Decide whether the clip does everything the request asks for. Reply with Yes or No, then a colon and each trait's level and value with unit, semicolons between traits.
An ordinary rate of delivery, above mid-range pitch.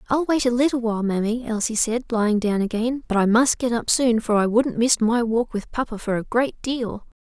No: fast, 240 wpm; high, 230 Hz